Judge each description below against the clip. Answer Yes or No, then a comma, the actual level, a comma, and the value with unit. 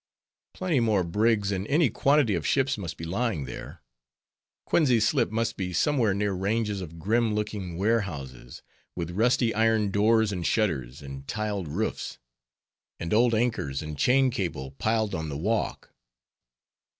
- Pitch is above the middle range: No, low, 105 Hz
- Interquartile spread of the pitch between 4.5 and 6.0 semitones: Yes, average, 5.1 semitones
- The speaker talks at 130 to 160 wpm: Yes, average, 150 wpm